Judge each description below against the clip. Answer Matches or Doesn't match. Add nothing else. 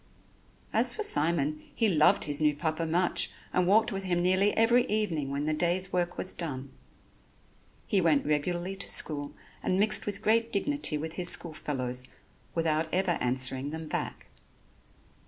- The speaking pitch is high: Doesn't match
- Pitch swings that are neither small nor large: Matches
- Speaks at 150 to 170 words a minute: Matches